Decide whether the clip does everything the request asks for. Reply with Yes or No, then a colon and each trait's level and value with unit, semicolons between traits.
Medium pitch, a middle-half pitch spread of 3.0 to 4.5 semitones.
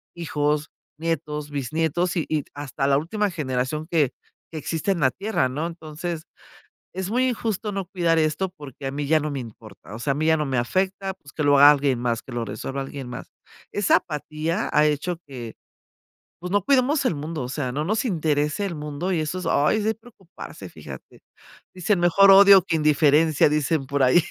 Yes: medium, 155 Hz; average, 4.2 semitones